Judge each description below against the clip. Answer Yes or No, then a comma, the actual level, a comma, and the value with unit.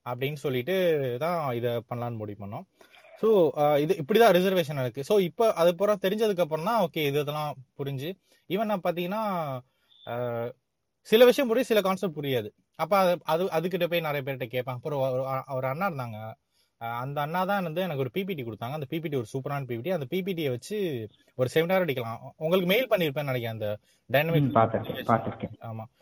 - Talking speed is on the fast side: Yes, fast, 165 wpm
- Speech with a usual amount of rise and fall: No, wide, 6.7 semitones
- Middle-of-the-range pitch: Yes, medium, 150 Hz